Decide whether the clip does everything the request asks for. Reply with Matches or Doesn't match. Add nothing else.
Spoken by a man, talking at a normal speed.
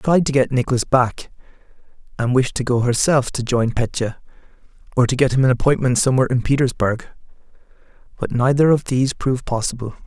Matches